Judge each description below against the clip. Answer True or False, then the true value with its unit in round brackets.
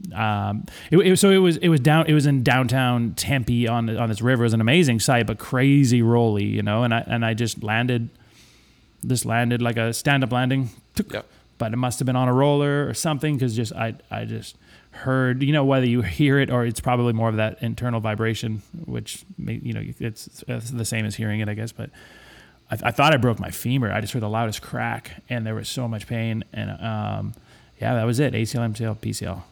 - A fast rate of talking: True (230 wpm)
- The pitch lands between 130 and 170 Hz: False (120 Hz)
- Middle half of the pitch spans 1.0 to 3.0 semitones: True (2.7 semitones)